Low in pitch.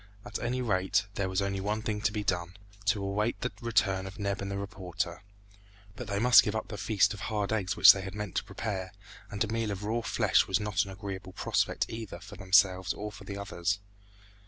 Yes: low, 100 Hz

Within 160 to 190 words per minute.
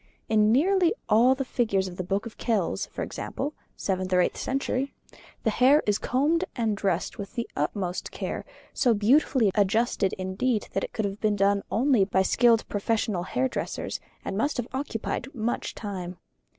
Yes: average, 170 wpm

